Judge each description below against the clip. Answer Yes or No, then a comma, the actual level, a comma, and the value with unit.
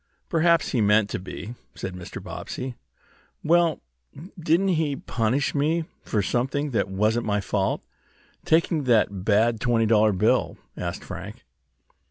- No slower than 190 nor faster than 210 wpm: No, slow, 135 wpm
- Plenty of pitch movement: Yes, wide, 6.7 semitones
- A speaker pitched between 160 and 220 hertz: No, low, 120 Hz